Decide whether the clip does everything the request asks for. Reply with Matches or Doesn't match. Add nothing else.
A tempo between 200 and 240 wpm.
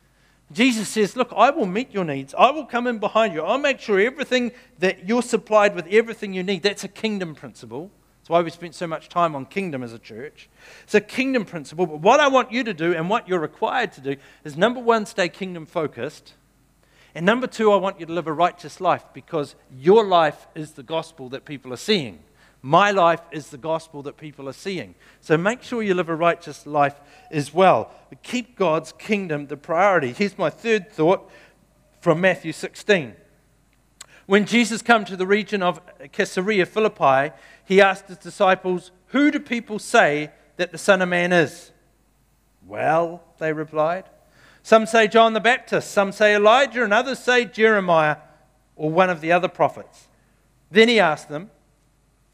Doesn't match